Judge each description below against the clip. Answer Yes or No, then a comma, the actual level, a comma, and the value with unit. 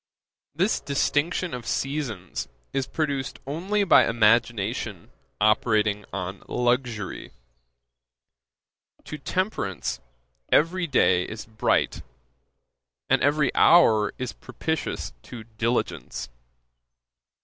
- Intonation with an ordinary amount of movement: No, wide, 5.9 semitones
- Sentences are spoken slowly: Yes, slow, 85 wpm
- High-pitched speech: No, low, 120 Hz